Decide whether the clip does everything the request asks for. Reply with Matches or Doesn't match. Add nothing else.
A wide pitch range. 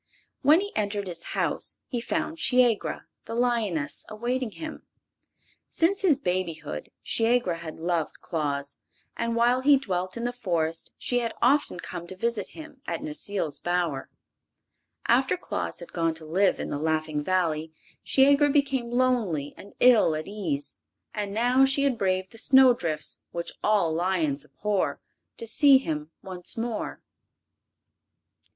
Matches